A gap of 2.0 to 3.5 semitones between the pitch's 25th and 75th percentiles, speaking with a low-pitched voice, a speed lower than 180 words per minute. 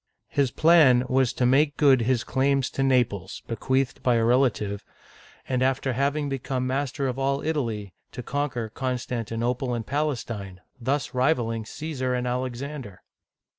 Yes: narrow, 2.6 semitones; low, 130 Hz; average, 150 wpm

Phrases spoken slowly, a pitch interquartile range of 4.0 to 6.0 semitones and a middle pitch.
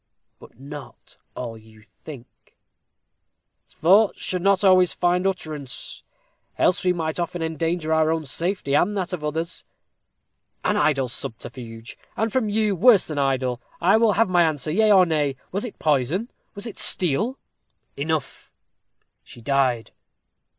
No: average, 145 wpm; wide, 5.4 semitones; medium, 160 Hz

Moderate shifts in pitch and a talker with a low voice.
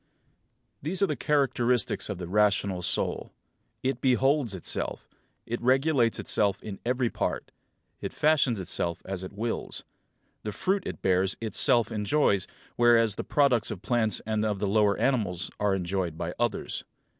Yes: average, 4.5 semitones; low, 110 Hz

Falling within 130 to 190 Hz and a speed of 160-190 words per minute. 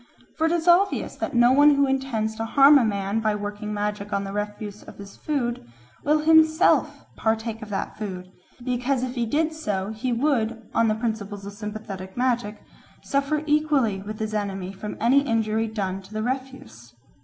No: high, 220 Hz; average, 185 wpm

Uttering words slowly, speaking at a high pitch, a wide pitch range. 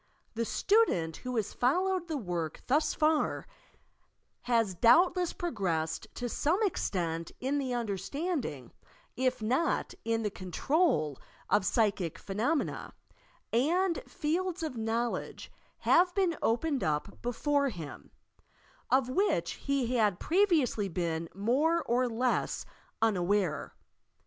Yes: slow, 115 wpm; high, 245 Hz; wide, 8.1 semitones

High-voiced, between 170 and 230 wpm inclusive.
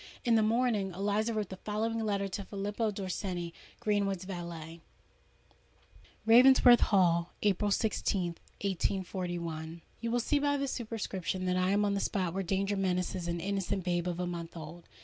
No: high, 195 Hz; average, 160 wpm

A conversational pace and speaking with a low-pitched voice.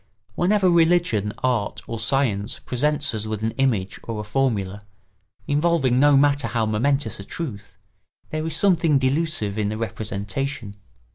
Yes: average, 145 wpm; low, 125 Hz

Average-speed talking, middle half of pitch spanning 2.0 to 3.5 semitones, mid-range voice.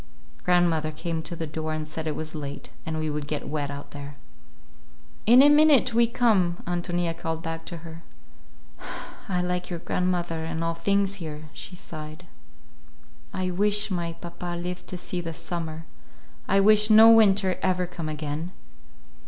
Yes: average, 165 wpm; average, 2.9 semitones; medium, 175 Hz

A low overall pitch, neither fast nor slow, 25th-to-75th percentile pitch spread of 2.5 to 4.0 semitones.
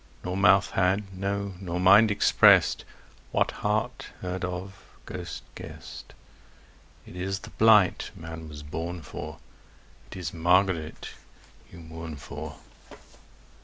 No: very low, 90 Hz; slow, 120 wpm; average, 2.8 semitones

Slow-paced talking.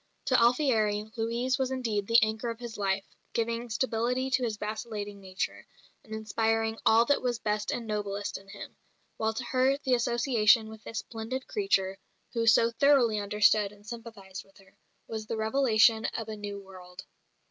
No: average, 170 wpm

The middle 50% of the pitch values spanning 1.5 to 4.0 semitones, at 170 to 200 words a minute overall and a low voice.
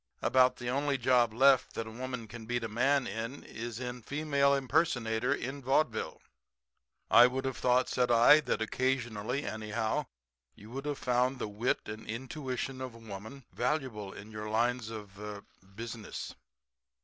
No: average, 3.0 semitones; average, 160 wpm; low, 120 Hz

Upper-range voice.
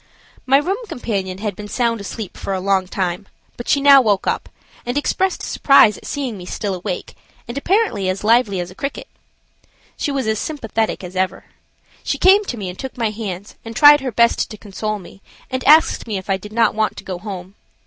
Yes: high, 215 Hz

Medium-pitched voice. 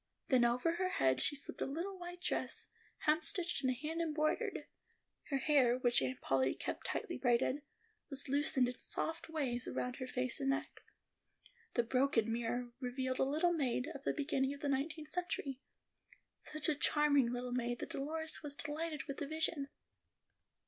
No: very high, 275 Hz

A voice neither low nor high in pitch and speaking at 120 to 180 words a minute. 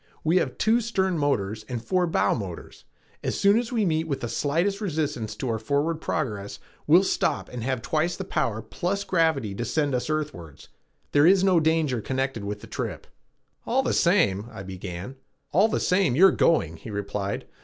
No: medium, 145 Hz; average, 195 wpm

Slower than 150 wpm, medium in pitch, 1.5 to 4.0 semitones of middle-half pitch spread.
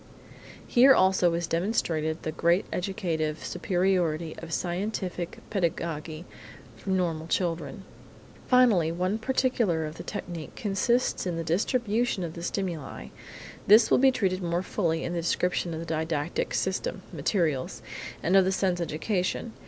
Yes: average, 140 wpm; medium, 175 Hz; average, 3.0 semitones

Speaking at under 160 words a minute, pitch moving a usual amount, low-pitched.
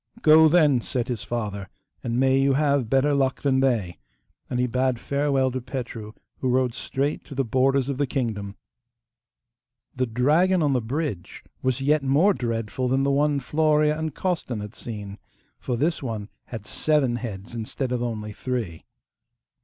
No: average, 170 wpm; average, 3.4 semitones; low, 130 Hz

